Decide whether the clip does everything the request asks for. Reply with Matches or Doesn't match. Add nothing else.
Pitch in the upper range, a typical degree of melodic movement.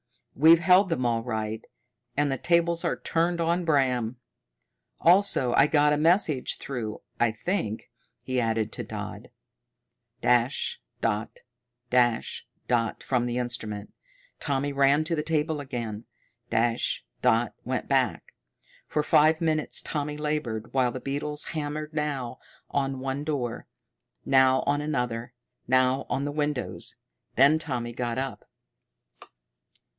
Doesn't match